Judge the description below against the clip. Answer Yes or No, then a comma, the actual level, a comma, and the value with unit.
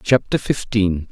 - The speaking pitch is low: Yes, low, 100 Hz